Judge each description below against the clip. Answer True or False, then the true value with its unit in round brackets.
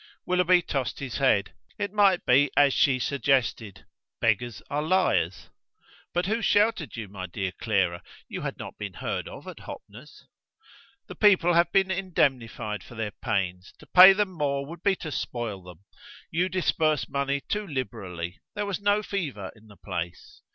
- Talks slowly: False (165 wpm)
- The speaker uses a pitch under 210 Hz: True (140 Hz)